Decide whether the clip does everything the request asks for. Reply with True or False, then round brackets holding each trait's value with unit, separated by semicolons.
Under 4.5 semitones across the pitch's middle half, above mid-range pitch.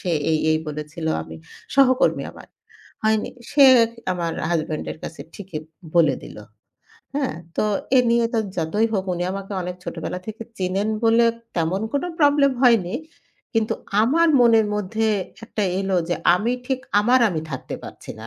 False (5.5 semitones; 205 Hz)